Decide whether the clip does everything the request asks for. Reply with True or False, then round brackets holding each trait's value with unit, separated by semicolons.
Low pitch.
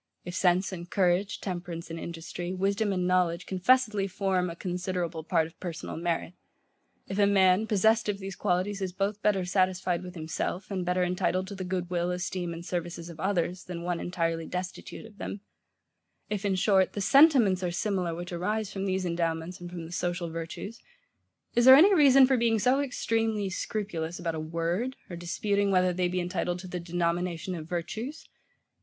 False (180 Hz)